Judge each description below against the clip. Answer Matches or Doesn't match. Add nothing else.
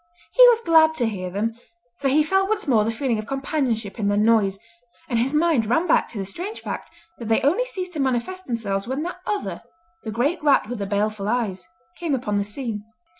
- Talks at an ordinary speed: Doesn't match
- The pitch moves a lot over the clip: Matches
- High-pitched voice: Matches